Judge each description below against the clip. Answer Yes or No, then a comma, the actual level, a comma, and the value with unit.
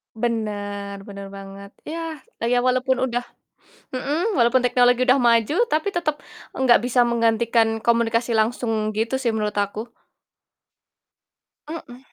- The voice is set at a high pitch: Yes, high, 235 Hz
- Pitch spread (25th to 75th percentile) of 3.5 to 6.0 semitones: No, average, 2.8 semitones